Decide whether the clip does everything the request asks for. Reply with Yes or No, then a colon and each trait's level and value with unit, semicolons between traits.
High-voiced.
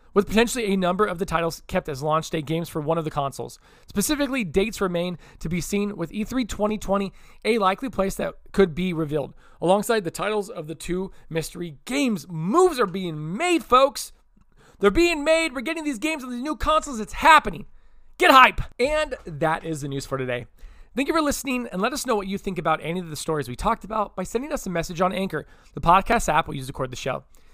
Yes: high, 195 Hz